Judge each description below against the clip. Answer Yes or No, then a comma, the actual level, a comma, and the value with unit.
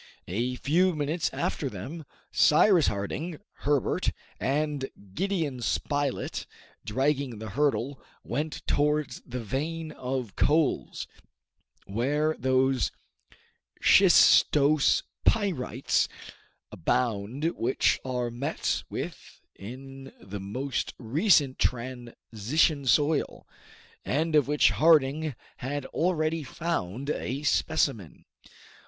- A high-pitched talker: No, medium, 140 Hz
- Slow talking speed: Yes, slow, 90 wpm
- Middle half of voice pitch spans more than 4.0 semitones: No, average, 3.6 semitones